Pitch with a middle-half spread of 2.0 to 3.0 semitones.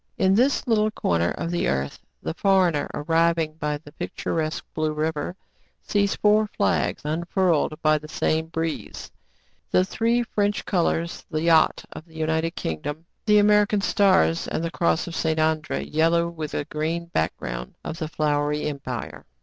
No: average, 3.4 semitones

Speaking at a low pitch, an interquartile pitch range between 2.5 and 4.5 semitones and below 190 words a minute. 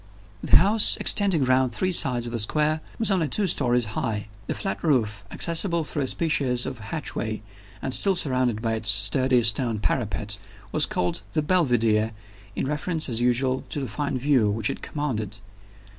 No: low, 130 Hz; wide, 5.5 semitones; average, 175 wpm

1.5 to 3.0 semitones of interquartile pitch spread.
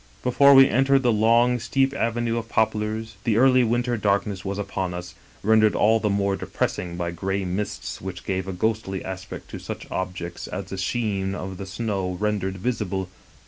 No: average, 3.4 semitones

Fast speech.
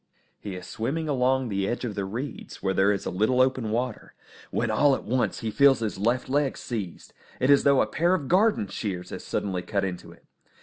Yes: fast, 225 wpm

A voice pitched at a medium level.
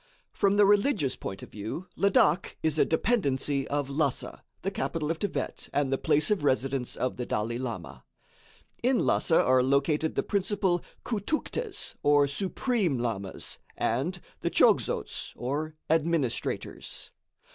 Yes: medium, 150 Hz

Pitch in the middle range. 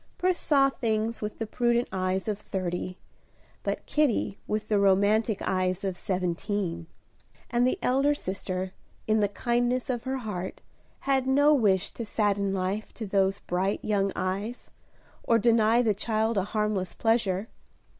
No: high, 210 Hz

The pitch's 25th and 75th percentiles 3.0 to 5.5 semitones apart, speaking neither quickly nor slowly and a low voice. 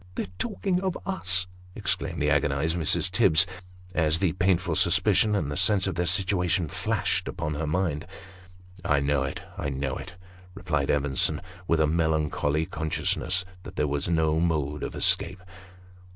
Yes: average, 3.5 semitones; average, 170 wpm; very low, 80 Hz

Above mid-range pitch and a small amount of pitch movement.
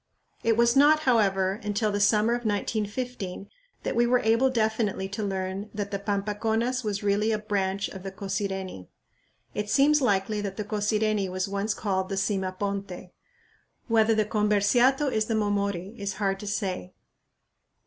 Yes: high, 205 Hz; narrow, 2.1 semitones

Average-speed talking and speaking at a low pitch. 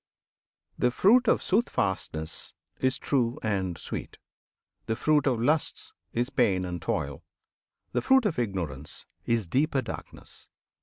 No: slow, 125 wpm; low, 115 Hz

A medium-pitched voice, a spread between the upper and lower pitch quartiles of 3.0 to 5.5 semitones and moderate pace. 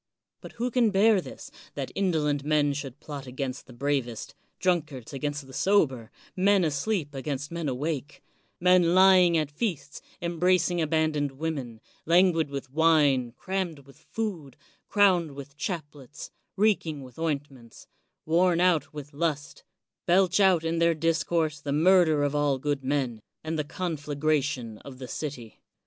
Yes: medium, 150 Hz; average, 3.8 semitones; average, 155 wpm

